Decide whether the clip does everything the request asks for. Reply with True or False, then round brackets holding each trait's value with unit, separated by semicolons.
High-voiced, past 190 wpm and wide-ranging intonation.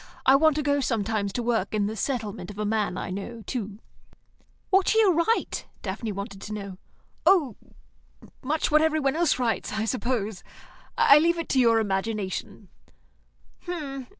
False (230 Hz; 165 wpm; 6.0 semitones)